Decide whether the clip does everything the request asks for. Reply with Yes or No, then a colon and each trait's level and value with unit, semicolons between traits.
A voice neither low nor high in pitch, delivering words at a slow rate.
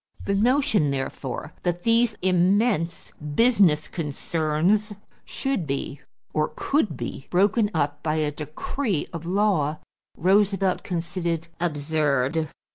Yes: medium, 170 Hz; slow, 110 wpm